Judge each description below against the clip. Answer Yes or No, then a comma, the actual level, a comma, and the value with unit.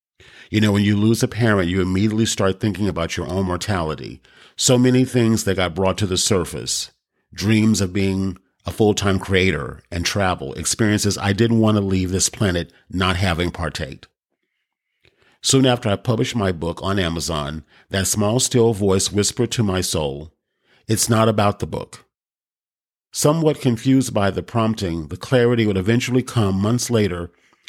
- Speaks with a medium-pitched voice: No, low, 100 Hz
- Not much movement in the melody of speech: No, average, 3.7 semitones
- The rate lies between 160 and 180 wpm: Yes, average, 165 wpm